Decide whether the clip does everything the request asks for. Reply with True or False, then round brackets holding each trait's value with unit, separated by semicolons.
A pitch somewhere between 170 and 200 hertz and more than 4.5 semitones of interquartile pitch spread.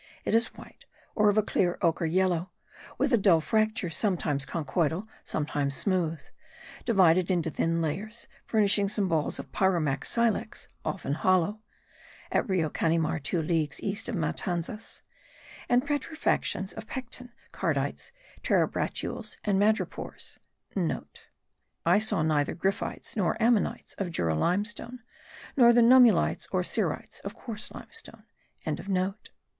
True (190 Hz; 4.9 semitones)